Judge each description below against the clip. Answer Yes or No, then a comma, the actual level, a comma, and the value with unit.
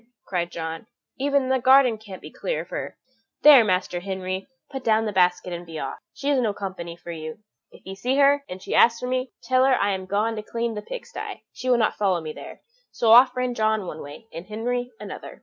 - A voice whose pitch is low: No, high, 215 Hz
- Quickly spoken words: Yes, fast, 235 wpm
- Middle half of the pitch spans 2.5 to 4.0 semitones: No, wide, 5.6 semitones